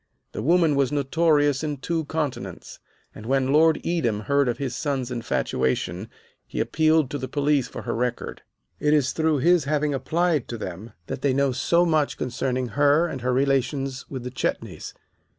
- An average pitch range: Yes, average, 3.3 semitones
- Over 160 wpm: Yes, average, 175 wpm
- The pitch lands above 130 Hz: Yes, medium, 140 Hz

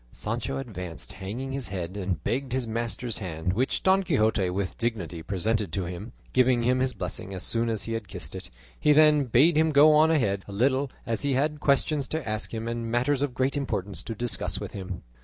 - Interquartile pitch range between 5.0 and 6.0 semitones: Yes, wide, 5.5 semitones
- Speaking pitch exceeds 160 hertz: No, low, 115 Hz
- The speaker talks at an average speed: No, fast, 215 wpm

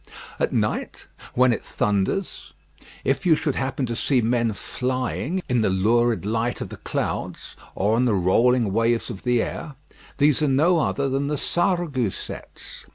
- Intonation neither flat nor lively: Yes, average, 3.9 semitones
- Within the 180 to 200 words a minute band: No, average, 160 wpm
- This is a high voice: No, low, 125 Hz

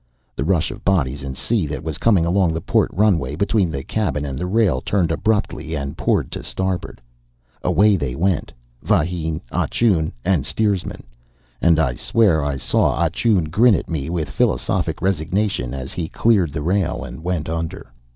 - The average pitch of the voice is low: Yes, very low, 85 Hz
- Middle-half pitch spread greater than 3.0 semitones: Yes, average, 4.9 semitones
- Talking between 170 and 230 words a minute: Yes, average, 180 wpm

